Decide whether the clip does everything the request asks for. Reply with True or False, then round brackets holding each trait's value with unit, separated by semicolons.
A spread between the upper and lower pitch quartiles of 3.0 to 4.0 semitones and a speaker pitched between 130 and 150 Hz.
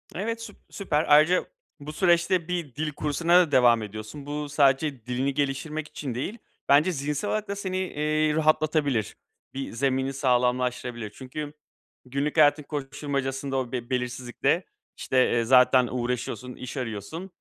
True (3.6 semitones; 140 Hz)